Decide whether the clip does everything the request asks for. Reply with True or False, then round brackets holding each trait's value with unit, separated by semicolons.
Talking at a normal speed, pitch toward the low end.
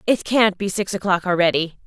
False (195 wpm; 195 Hz)